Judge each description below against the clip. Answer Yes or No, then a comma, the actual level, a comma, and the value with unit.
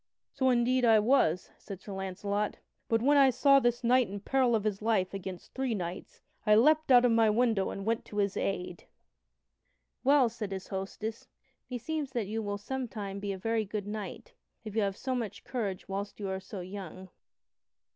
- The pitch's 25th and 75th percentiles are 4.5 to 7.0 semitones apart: No, average, 3.9 semitones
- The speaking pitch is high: Yes, high, 215 Hz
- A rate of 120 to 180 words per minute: No, average, 190 wpm